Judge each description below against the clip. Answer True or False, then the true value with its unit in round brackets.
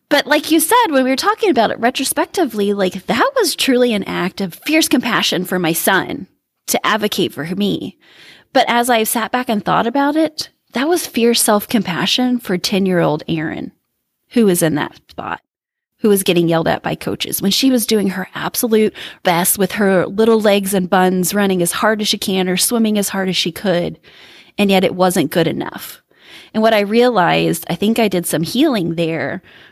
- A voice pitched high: True (210 Hz)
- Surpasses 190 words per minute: True (200 wpm)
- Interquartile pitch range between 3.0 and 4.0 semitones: False (5.2 semitones)